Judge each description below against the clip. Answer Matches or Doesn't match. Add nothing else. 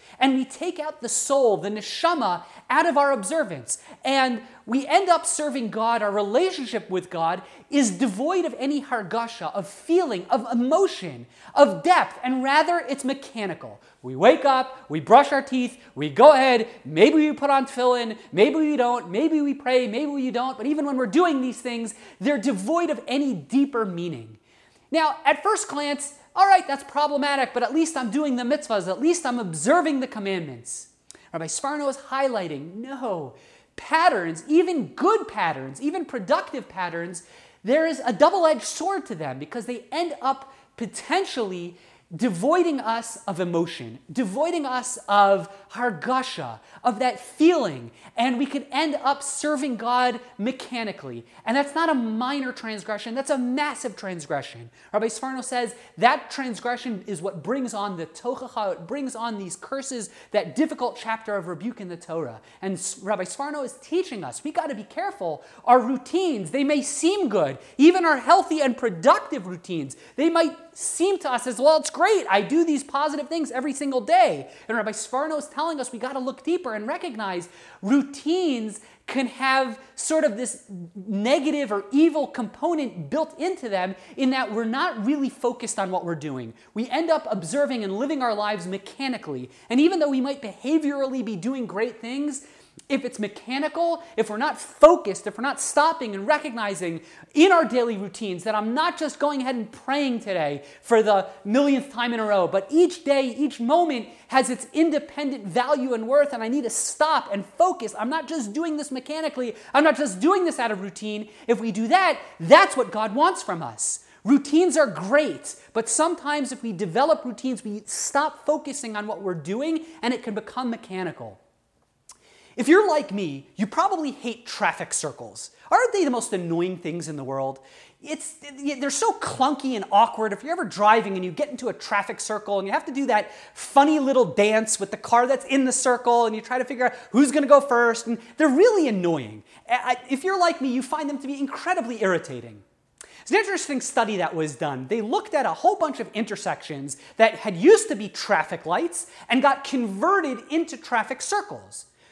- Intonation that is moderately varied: Doesn't match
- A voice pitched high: Matches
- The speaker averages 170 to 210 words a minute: Matches